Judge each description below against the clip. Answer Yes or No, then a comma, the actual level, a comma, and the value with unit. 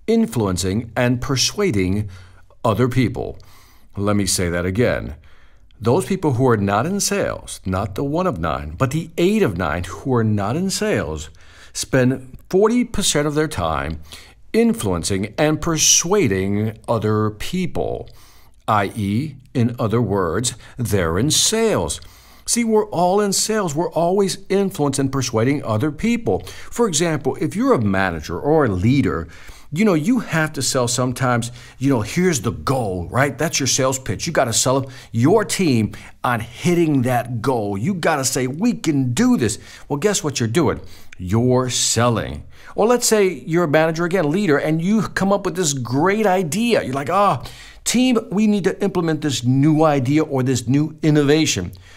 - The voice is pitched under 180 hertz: Yes, low, 135 Hz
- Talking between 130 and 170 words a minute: Yes, average, 165 wpm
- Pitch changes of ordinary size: No, wide, 8.3 semitones